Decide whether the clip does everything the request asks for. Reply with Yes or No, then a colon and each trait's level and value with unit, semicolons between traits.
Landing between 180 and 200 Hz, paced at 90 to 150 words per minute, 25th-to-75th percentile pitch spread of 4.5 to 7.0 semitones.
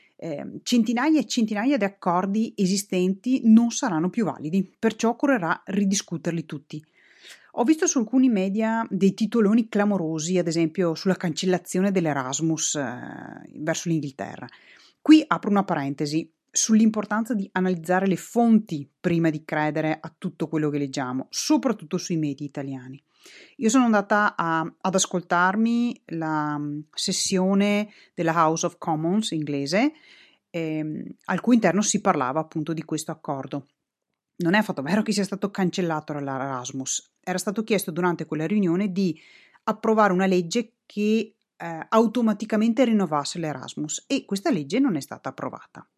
Yes: medium, 185 Hz; average, 140 wpm; wide, 5.4 semitones